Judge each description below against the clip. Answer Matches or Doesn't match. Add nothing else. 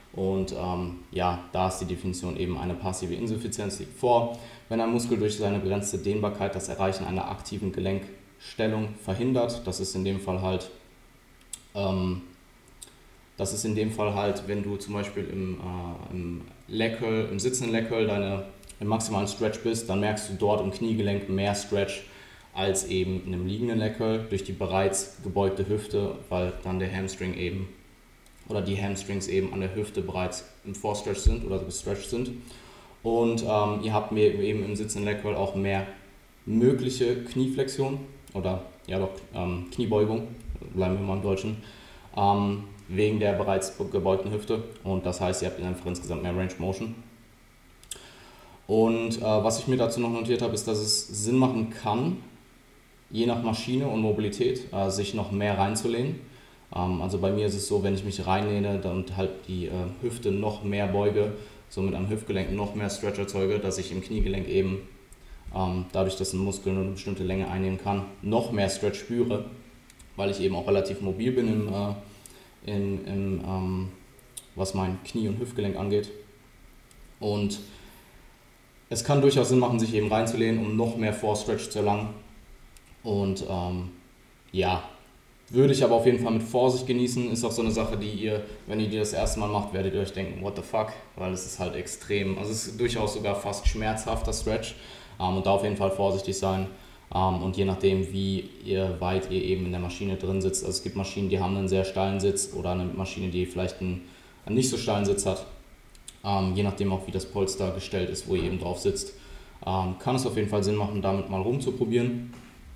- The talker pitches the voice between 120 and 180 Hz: Doesn't match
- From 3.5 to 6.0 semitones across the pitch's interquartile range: Doesn't match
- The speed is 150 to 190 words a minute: Matches